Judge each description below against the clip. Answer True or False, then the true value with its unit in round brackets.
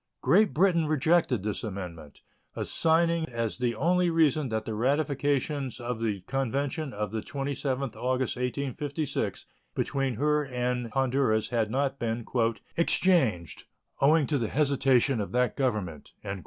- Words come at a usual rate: False (130 wpm)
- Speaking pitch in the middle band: False (130 Hz)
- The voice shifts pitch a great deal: False (4.3 semitones)